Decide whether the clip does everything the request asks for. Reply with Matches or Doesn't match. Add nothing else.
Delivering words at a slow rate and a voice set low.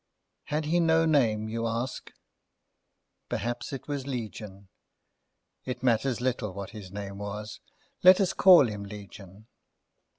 Matches